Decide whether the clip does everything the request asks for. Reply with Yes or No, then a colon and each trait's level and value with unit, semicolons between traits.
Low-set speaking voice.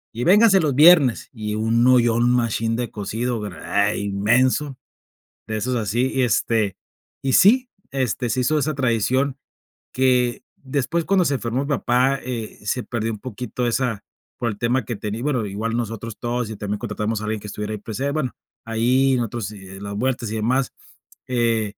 Yes: low, 120 Hz